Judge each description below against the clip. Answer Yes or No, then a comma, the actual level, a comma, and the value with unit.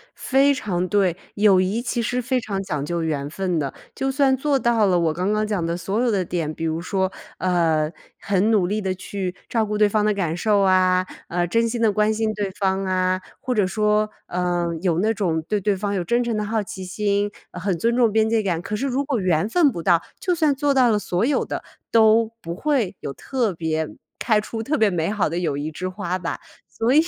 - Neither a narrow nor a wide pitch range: Yes, average, 4.0 semitones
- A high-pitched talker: Yes, high, 200 Hz